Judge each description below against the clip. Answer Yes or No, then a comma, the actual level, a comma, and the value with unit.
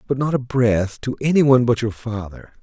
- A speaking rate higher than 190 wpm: Yes, fast, 205 wpm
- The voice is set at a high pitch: No, low, 125 Hz